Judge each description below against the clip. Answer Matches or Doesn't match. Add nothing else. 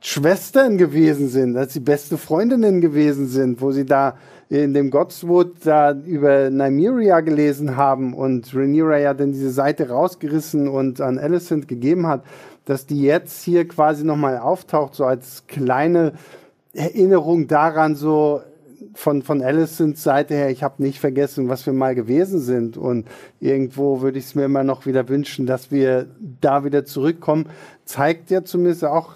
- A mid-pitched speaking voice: Matches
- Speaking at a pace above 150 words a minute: Matches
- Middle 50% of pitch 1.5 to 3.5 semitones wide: Matches